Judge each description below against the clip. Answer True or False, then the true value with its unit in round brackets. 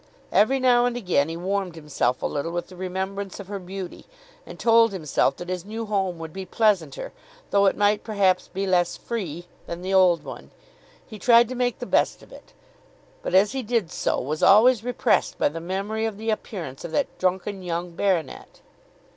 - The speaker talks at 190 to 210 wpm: True (195 wpm)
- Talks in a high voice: True (195 Hz)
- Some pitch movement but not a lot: True (3.8 semitones)